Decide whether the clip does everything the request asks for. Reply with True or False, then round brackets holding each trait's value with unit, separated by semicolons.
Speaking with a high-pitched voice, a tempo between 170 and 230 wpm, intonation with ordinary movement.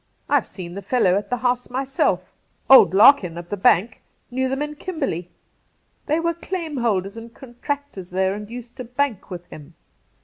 False (240 Hz; 175 wpm; 6.1 semitones)